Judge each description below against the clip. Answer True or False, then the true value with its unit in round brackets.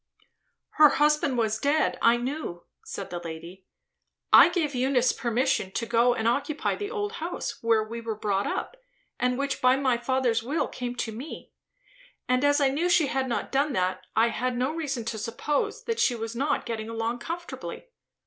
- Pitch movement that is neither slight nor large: True (4.0 semitones)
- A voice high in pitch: True (250 Hz)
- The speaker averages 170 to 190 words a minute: True (185 wpm)